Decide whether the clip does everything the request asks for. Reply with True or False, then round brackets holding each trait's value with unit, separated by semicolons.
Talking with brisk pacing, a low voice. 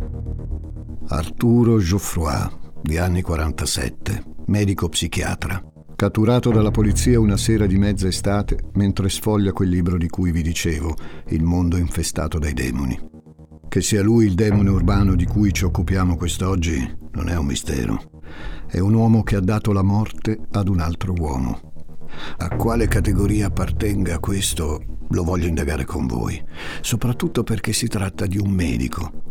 False (145 wpm; 90 Hz)